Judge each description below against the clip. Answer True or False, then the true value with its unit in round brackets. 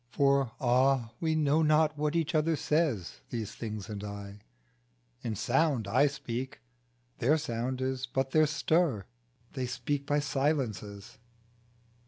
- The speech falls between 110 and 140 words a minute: True (135 wpm)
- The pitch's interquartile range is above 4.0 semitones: True (4.6 semitones)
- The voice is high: False (135 Hz)